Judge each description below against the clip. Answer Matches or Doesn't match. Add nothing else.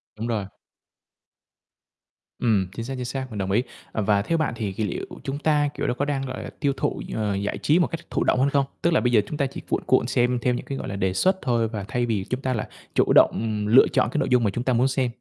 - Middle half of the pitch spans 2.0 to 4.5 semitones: Matches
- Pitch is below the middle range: Matches